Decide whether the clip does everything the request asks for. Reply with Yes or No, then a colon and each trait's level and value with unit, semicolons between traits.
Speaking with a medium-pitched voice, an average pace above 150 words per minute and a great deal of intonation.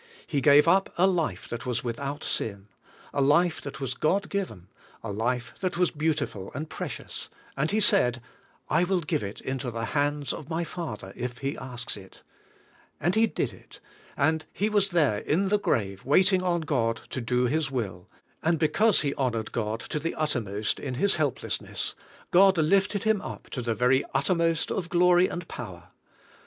Yes: medium, 145 Hz; average, 180 wpm; wide, 6.4 semitones